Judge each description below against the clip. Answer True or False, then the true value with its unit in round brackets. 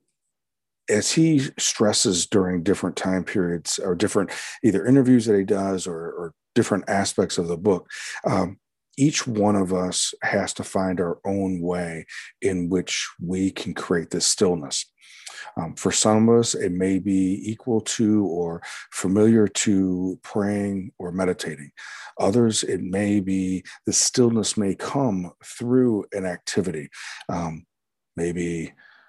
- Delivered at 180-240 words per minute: False (140 wpm)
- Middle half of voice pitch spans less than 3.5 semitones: True (3.1 semitones)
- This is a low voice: True (95 Hz)